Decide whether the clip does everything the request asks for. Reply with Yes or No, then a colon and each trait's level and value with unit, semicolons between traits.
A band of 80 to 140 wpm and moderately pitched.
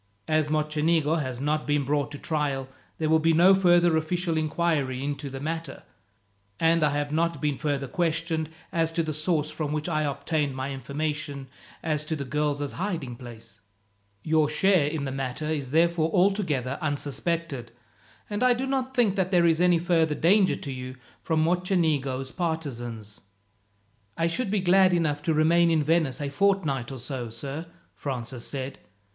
No: average, 170 wpm; medium, 155 Hz